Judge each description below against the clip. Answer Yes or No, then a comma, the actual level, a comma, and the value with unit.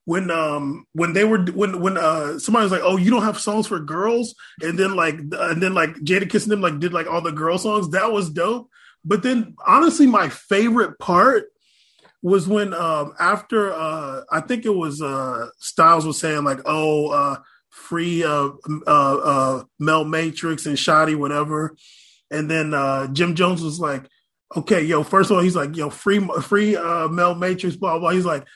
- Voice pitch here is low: No, medium, 170 Hz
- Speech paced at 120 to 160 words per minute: No, average, 195 wpm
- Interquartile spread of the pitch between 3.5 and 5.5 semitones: Yes, average, 4.7 semitones